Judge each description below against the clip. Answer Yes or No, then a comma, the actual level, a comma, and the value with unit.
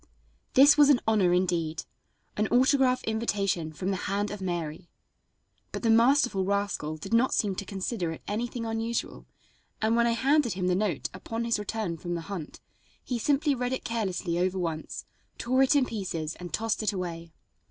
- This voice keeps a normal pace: Yes, average, 180 wpm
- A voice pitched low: No, high, 205 Hz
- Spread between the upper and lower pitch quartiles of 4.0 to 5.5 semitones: Yes, average, 4.7 semitones